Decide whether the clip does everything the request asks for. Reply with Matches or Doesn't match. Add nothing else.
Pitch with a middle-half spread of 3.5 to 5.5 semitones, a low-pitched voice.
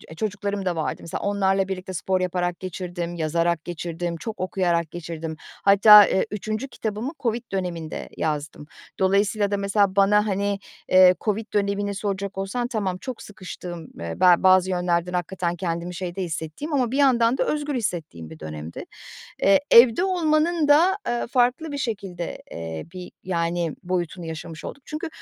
Doesn't match